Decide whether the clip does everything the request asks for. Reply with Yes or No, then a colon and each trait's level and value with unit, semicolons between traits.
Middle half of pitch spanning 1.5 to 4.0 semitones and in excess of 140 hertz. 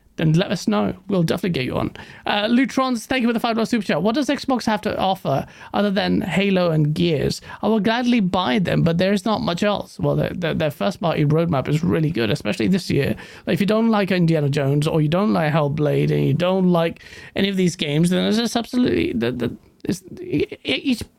No: average, 5.2 semitones; high, 190 Hz